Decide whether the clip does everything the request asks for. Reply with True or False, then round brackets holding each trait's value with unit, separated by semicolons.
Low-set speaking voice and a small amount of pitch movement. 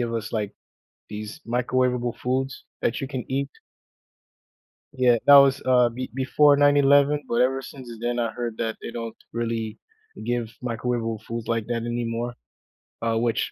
True (120 Hz; 2.2 semitones)